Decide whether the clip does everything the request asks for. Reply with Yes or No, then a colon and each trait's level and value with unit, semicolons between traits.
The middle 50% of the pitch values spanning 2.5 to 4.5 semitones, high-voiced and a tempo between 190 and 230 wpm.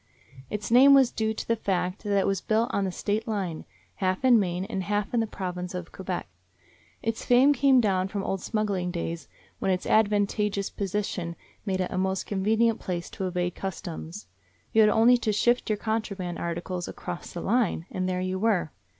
Yes: average, 3.1 semitones; high, 195 Hz; average, 195 wpm